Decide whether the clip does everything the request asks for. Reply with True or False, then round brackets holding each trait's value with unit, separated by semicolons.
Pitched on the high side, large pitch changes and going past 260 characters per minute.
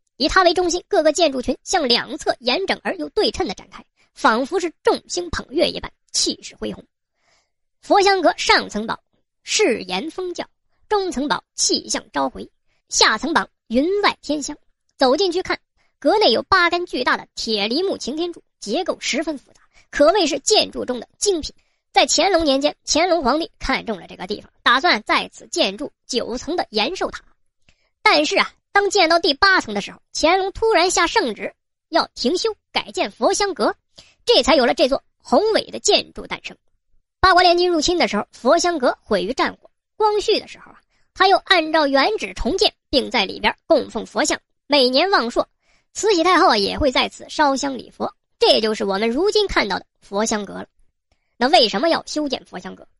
False (335 Hz; 5.0 semitones; 270 characters per minute)